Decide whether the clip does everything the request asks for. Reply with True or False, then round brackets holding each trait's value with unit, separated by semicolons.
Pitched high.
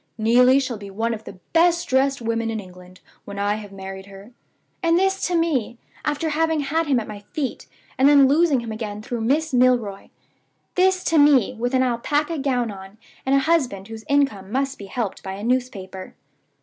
True (245 Hz)